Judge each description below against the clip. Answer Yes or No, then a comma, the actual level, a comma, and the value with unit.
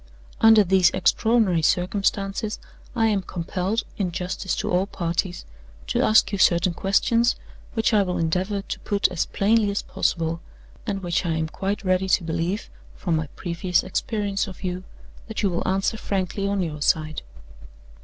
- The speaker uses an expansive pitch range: No, average, 2.7 semitones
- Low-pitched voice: No, high, 190 Hz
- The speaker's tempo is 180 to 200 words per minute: No, average, 165 wpm